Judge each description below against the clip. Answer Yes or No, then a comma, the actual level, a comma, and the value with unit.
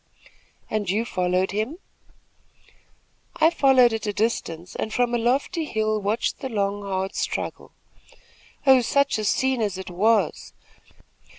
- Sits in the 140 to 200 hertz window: No, high, 215 Hz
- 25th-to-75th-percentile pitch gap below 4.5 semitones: Yes, average, 3.9 semitones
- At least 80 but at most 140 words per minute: Yes, slow, 135 wpm